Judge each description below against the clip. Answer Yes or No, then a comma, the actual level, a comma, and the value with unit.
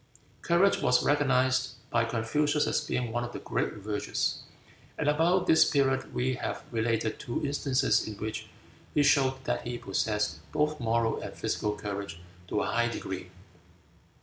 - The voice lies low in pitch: Yes, low, 120 Hz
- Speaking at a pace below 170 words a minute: Yes, average, 155 wpm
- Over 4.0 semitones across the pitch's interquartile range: Yes, average, 4.6 semitones